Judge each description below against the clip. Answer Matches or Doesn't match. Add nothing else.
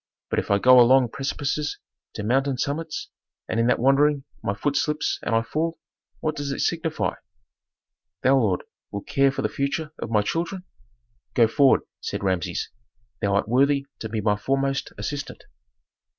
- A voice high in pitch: Doesn't match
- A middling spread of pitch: Matches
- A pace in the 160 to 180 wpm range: Matches